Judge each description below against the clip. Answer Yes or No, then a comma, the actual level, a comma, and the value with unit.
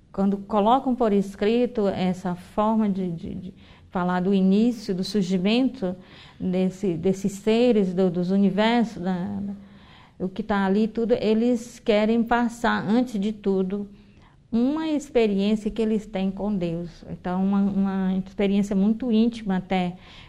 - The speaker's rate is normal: Yes, average, 140 wpm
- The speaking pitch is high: Yes, high, 200 Hz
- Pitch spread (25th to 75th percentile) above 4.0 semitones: No, average, 2.8 semitones